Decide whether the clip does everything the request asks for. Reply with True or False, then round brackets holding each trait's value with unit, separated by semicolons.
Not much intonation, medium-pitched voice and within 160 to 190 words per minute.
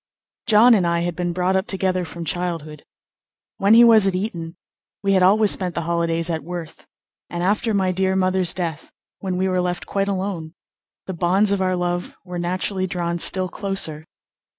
True (2.0 semitones; 180 Hz; 185 wpm)